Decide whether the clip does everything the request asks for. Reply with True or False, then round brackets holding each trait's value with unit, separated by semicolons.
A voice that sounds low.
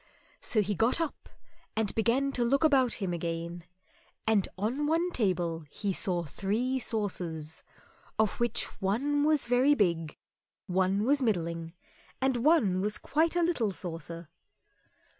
False (215 Hz)